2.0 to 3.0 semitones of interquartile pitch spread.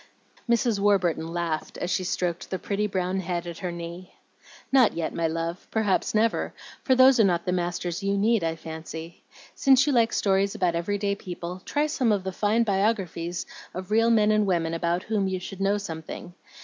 No: average, 3.6 semitones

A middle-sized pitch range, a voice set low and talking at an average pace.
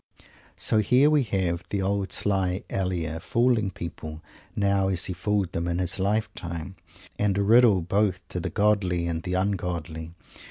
Yes: average, 3.0 semitones; very low, 95 Hz; average, 160 wpm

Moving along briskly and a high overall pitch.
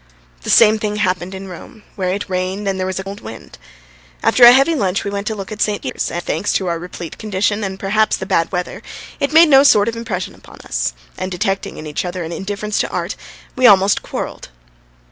Yes: fast, 225 wpm; high, 195 Hz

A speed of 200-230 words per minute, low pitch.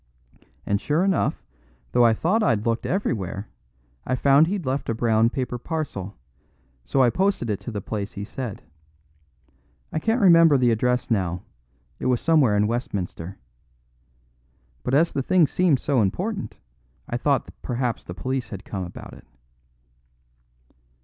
No: average, 150 wpm; low, 125 Hz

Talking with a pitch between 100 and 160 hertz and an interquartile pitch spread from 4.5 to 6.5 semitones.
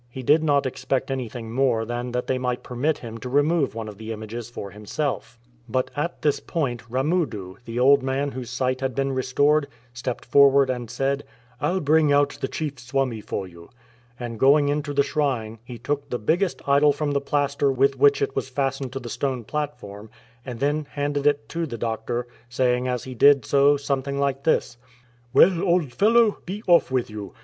No: low, 135 Hz; average, 3.0 semitones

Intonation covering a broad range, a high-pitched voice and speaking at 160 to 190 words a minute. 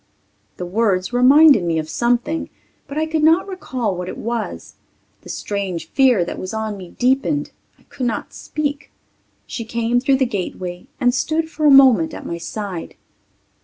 Yes: wide, 6.8 semitones; high, 240 Hz; average, 170 wpm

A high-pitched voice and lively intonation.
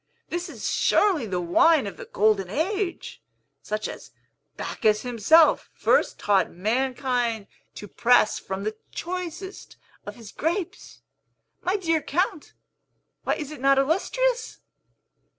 Yes: very high, 270 Hz; wide, 8.4 semitones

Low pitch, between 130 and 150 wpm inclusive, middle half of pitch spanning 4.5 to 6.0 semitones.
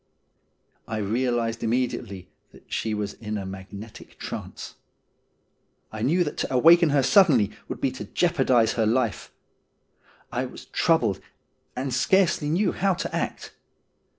Yes: low, 125 Hz; slow, 135 wpm; wide, 5.5 semitones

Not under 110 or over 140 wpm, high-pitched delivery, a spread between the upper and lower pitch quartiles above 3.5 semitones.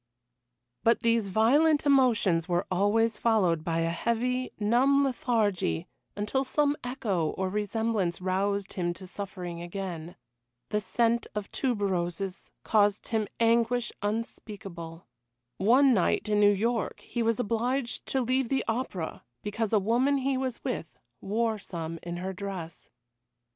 Yes: slow, 135 wpm; high, 210 Hz; average, 4.2 semitones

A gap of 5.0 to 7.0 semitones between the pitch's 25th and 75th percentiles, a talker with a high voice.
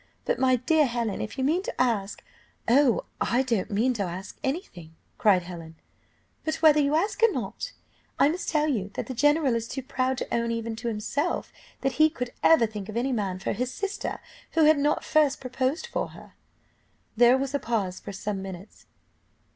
Yes: wide, 5.5 semitones; very high, 250 Hz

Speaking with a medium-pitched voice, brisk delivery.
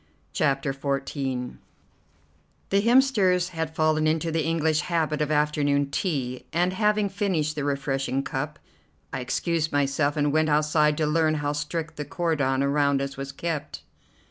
No: medium, 150 Hz; average, 145 wpm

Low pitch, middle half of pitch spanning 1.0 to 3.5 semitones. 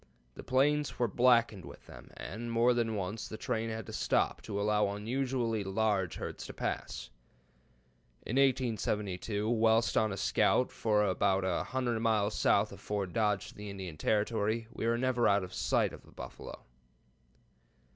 Yes: low, 110 Hz; average, 2.7 semitones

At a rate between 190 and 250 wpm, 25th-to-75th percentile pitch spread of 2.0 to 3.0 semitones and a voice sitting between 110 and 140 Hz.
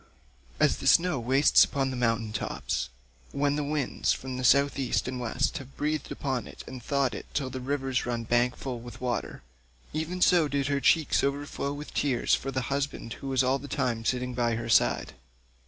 Yes: average, 195 wpm; narrow, 2.5 semitones; low, 135 Hz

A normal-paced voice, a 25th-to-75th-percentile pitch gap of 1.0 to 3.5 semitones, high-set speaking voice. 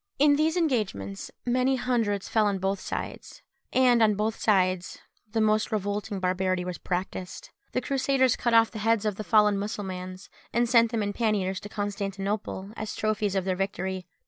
Yes: average, 170 wpm; average, 3.2 semitones; high, 210 Hz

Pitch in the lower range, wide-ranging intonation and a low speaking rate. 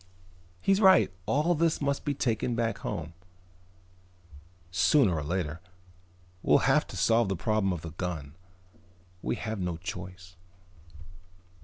Yes: very low, 95 Hz; wide, 6.4 semitones; slow, 130 wpm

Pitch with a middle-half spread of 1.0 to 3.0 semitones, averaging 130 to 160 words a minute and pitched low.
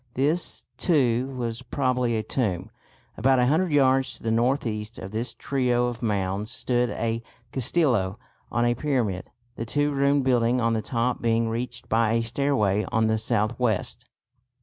No: narrow, 2.6 semitones; average, 170 wpm; low, 120 Hz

